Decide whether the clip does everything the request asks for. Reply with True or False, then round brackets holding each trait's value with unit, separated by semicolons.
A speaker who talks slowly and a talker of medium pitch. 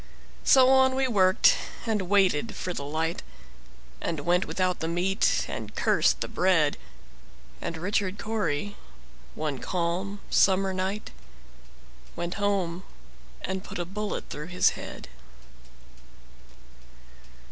True (105 wpm; 180 Hz)